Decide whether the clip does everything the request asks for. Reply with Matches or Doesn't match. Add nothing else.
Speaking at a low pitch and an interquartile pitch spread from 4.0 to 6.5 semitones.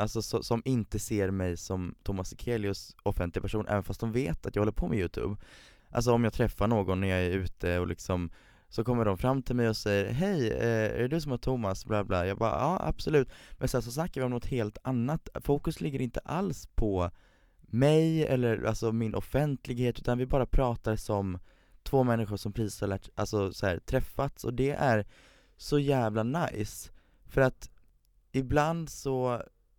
Matches